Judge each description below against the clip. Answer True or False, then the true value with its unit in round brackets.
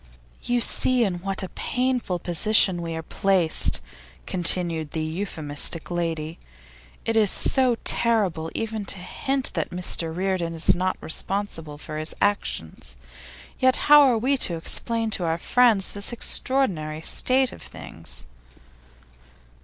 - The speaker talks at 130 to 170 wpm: True (135 wpm)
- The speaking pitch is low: False (185 Hz)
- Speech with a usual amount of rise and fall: False (5.8 semitones)